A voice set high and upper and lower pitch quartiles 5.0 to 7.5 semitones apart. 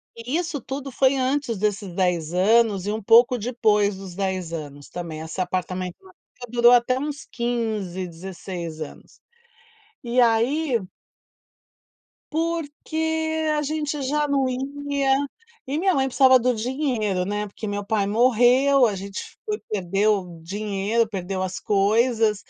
Yes: high, 225 Hz; wide, 5.6 semitones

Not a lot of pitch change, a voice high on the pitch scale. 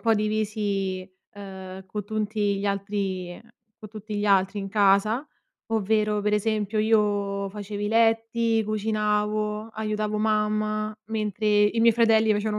Yes: narrow, 1.2 semitones; high, 210 Hz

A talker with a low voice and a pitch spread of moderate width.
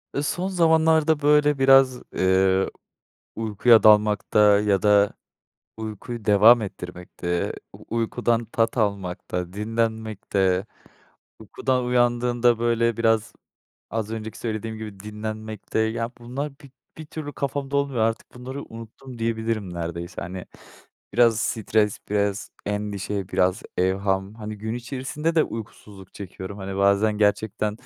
Yes: low, 110 Hz; average, 3.1 semitones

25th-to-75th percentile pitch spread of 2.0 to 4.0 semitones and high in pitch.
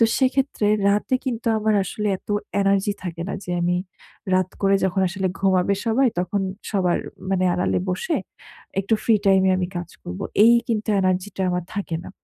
Yes: average, 2.9 semitones; high, 195 Hz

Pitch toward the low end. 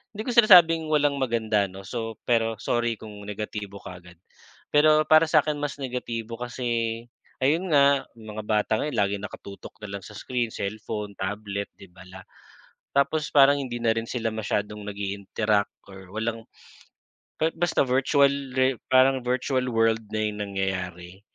Yes: low, 115 Hz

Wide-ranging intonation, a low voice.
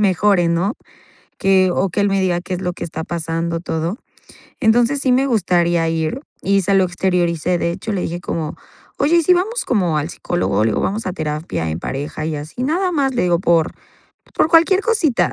No: wide, 6.0 semitones; medium, 180 Hz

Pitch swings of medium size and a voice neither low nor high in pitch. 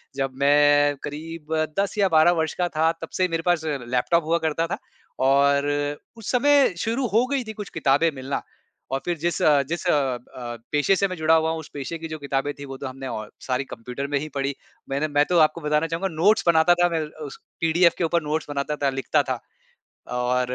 Yes: average, 3.4 semitones; medium, 155 Hz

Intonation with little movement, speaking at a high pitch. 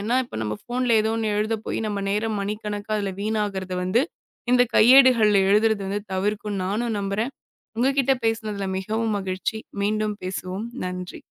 Yes: narrow, 2.2 semitones; high, 210 Hz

